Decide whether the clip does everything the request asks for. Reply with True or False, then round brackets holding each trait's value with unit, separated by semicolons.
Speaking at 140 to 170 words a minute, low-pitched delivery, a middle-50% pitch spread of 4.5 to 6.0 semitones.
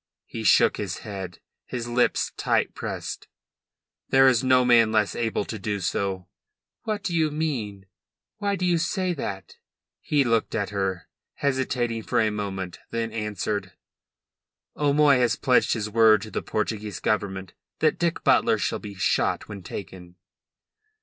True (155 wpm; 110 Hz; 4.8 semitones)